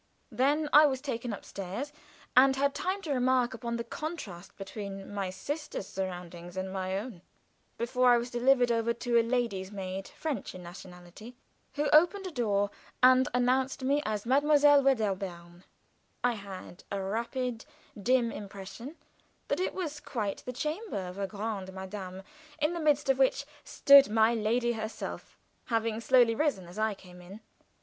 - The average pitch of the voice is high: Yes, high, 235 Hz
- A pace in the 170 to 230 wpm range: No, average, 160 wpm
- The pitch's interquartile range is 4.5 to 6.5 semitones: Yes, wide, 5.4 semitones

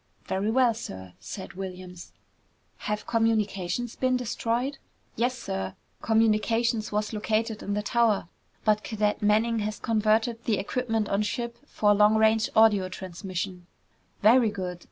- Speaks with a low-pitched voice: No, high, 215 Hz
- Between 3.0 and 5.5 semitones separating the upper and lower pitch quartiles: No, narrow, 2.4 semitones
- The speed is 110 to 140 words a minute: Yes, slow, 135 wpm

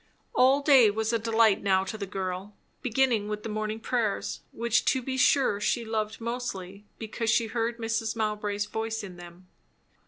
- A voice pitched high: Yes, high, 220 Hz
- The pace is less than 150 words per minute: No, average, 175 wpm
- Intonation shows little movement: Yes, narrow, 2.2 semitones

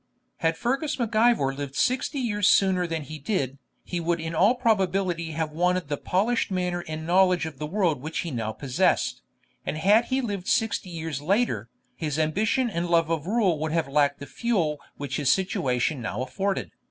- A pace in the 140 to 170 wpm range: No, average, 190 wpm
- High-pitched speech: No, medium, 170 Hz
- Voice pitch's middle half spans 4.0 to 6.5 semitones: Yes, average, 5.1 semitones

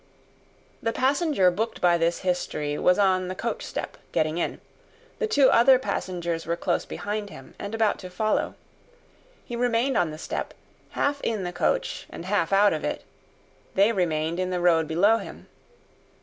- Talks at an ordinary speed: Yes, average, 165 wpm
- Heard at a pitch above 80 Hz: Yes, medium, 185 Hz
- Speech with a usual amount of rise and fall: Yes, average, 4.8 semitones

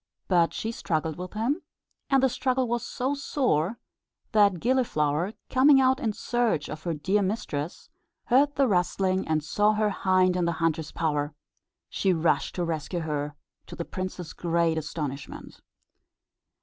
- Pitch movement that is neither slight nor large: No, wide, 6.7 semitones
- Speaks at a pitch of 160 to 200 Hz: Yes, medium, 185 Hz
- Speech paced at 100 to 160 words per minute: Yes, average, 150 wpm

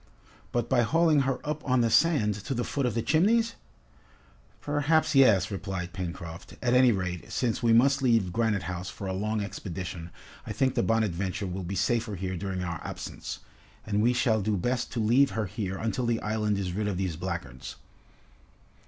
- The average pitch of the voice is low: Yes, low, 110 Hz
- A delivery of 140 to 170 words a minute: No, average, 190 wpm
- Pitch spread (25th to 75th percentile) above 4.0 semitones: Yes, average, 4.8 semitones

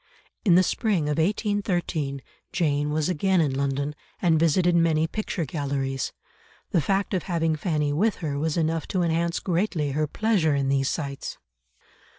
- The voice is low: No, medium, 160 Hz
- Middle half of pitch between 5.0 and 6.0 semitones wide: No, average, 3.6 semitones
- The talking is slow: No, average, 160 wpm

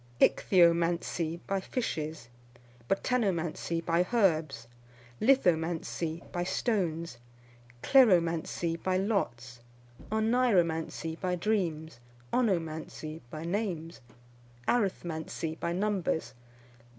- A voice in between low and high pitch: Yes, medium, 170 Hz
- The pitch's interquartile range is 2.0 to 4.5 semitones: Yes, average, 3.5 semitones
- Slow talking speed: Yes, slow, 75 wpm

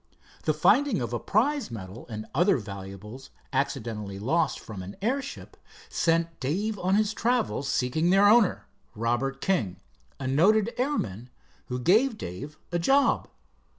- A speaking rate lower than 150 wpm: Yes, average, 140 wpm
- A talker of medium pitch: Yes, medium, 155 Hz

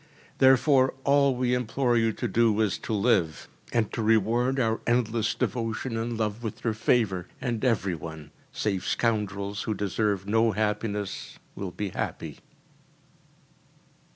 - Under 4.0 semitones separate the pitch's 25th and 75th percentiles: Yes, average, 2.8 semitones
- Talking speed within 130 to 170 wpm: Yes, average, 140 wpm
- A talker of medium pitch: No, low, 110 Hz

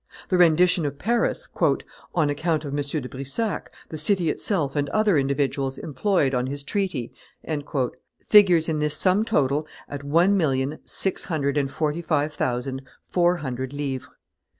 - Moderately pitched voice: Yes, medium, 150 Hz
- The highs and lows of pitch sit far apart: No, average, 4.2 semitones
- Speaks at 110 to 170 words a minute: Yes, average, 150 wpm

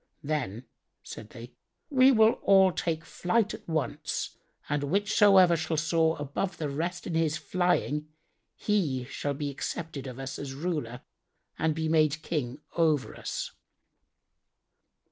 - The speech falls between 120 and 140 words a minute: Yes, slow, 135 wpm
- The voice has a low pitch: No, medium, 155 Hz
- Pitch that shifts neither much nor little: Yes, average, 3.8 semitones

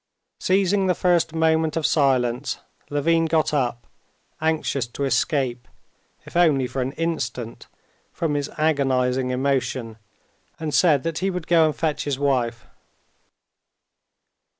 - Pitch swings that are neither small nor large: Yes, average, 4.1 semitones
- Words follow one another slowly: Yes, slow, 125 wpm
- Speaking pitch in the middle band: Yes, medium, 145 Hz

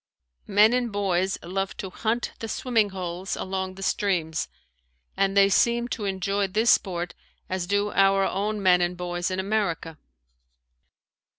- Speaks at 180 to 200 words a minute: No, average, 150 wpm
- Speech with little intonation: Yes, narrow, 2.2 semitones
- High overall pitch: Yes, high, 195 Hz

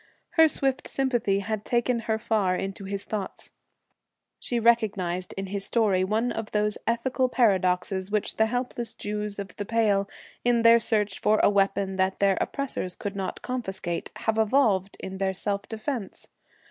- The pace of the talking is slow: No, average, 160 wpm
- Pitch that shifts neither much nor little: Yes, average, 3.2 semitones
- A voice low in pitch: No, high, 210 Hz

